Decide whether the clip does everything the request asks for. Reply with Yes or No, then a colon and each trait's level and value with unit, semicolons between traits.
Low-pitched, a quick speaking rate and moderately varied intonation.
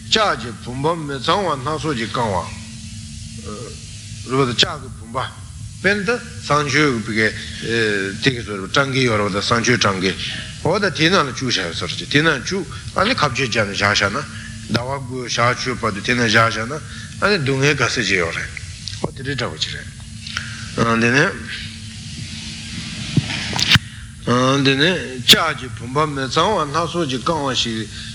Yes: low, 120 Hz; fast, 200 wpm; average, 4.1 semitones